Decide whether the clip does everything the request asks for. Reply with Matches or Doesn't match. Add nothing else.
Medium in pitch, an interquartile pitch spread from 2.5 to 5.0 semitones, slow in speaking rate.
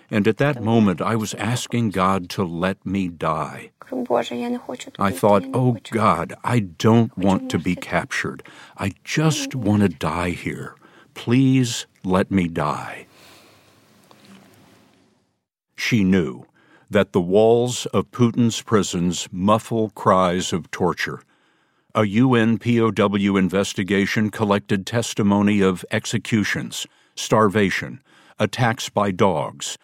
Doesn't match